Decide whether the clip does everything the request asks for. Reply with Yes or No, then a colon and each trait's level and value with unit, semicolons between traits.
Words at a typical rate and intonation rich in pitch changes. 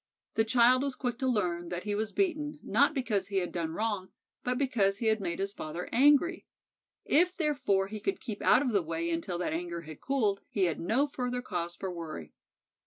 No: fast, 210 wpm; wide, 6.5 semitones